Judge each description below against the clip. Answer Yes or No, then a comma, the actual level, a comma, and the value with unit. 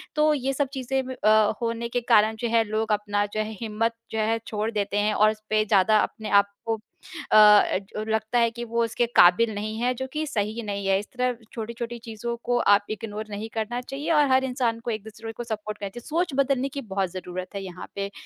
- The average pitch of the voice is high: Yes, high, 220 Hz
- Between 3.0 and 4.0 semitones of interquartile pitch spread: No, narrow, 2.4 semitones